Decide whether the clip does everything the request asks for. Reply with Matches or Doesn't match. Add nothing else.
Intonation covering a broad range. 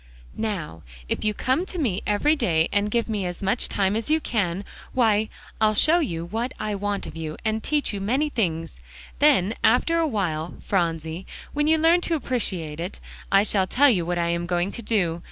Matches